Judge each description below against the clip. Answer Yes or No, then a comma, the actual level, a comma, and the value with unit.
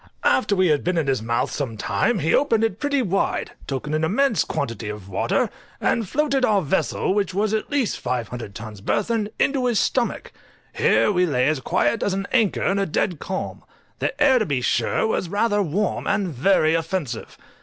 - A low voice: No, high, 190 Hz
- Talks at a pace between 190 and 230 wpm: Yes, average, 195 wpm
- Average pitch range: No, wide, 7.6 semitones